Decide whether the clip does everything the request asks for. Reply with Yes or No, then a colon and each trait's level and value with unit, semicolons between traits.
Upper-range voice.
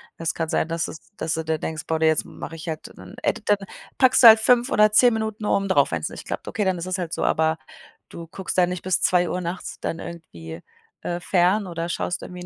No: medium, 175 Hz